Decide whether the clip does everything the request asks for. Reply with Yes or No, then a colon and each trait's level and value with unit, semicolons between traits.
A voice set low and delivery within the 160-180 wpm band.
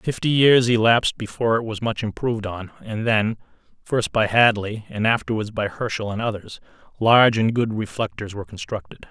Yes: low, 110 Hz; average, 170 wpm